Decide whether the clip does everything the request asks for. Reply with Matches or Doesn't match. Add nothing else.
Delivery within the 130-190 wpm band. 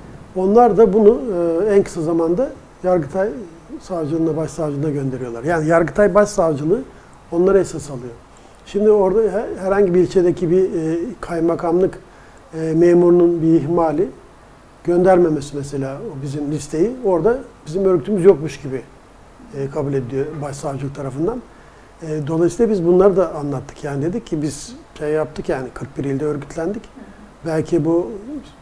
Doesn't match